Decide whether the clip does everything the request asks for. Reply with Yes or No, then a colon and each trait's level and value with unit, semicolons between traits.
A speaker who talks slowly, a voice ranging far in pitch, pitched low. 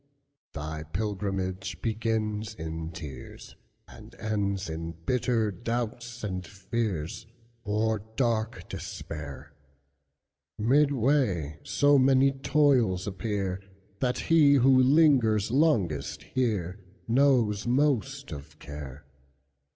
Yes: slow, 75 wpm; wide, 5.8 semitones; low, 105 Hz